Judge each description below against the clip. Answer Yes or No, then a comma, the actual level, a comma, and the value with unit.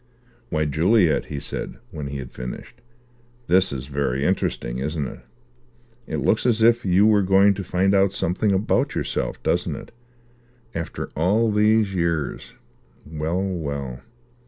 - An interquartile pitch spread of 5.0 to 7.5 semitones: Yes, average, 5.3 semitones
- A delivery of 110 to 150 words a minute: Yes, average, 145 wpm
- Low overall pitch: Yes, very low, 90 Hz